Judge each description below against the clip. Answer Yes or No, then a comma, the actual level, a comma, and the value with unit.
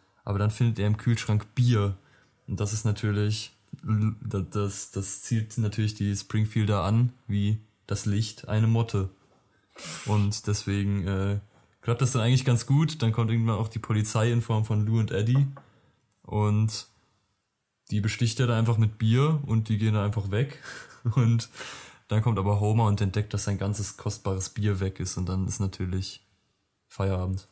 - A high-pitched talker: No, low, 105 Hz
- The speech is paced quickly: No, average, 170 wpm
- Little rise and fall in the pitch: Yes, narrow, 2.2 semitones